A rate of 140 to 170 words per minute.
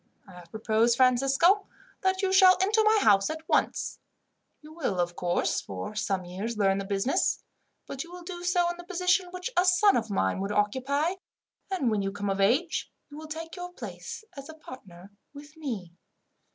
No: average, 190 wpm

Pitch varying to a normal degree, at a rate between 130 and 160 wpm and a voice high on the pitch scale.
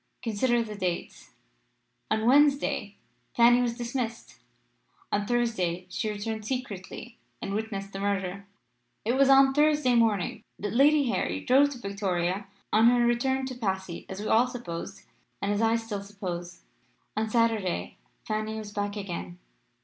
Yes: average, 3.5 semitones; average, 145 wpm; high, 220 Hz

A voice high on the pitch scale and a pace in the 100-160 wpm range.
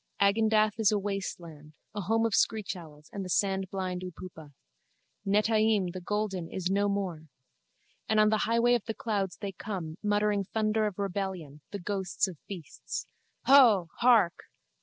Yes: high, 200 Hz; average, 155 wpm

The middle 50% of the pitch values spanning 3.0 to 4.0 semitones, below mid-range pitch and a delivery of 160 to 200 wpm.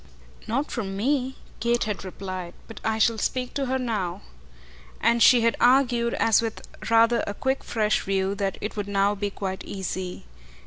No: average, 3.5 semitones; high, 220 Hz; average, 175 wpm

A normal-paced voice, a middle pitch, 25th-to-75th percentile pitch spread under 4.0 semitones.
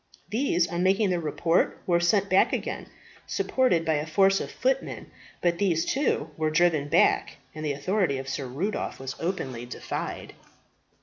No: average, 165 wpm; medium, 170 Hz; average, 4.3 semitones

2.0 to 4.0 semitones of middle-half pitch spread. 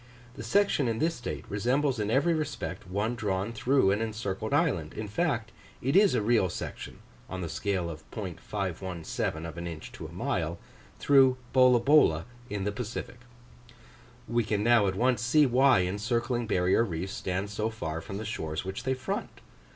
No: average, 5.0 semitones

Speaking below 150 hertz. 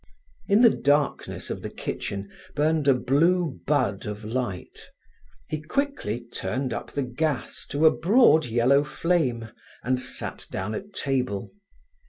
Yes: medium, 140 Hz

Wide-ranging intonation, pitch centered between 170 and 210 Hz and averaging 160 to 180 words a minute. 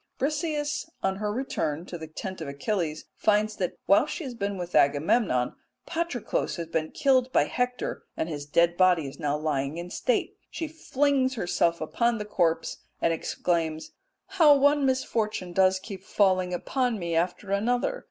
Yes: wide, 7.4 semitones; high, 190 Hz; average, 165 wpm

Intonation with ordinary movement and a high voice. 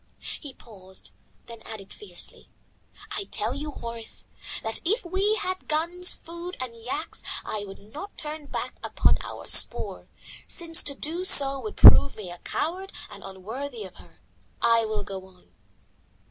No: wide, 7.9 semitones; very high, 275 Hz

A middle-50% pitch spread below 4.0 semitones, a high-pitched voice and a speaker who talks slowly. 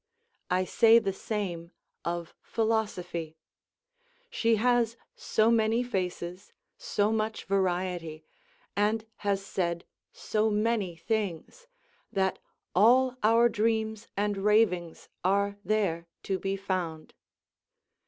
Yes: average, 3.6 semitones; high, 205 Hz; slow, 105 wpm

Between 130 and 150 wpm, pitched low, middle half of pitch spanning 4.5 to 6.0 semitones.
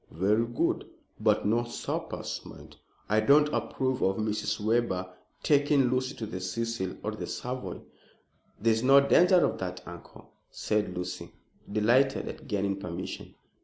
Yes: average, 145 wpm; low, 110 Hz; average, 5.1 semitones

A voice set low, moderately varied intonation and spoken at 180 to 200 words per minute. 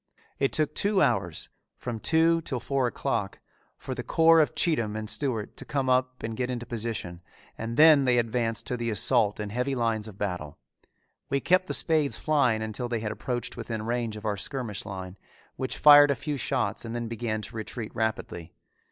Yes: low, 120 Hz; average, 4.0 semitones; average, 195 wpm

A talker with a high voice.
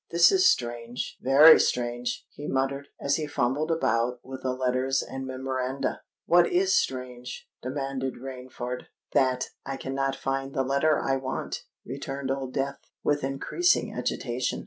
No: low, 135 Hz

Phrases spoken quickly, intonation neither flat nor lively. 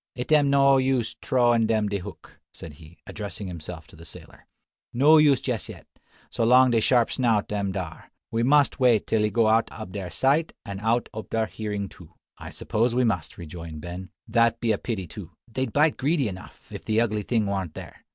Yes: fast, 210 wpm; average, 4.4 semitones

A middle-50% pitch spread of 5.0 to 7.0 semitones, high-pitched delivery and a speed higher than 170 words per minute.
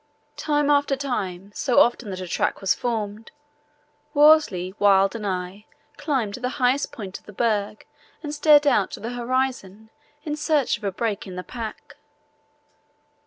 No: wide, 5.6 semitones; high, 230 Hz; average, 165 wpm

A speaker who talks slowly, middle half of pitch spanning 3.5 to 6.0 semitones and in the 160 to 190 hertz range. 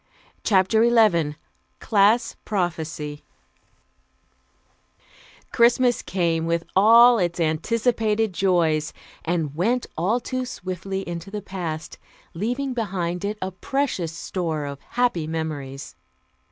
Yes: slow, 100 wpm; wide, 5.4 semitones; medium, 185 Hz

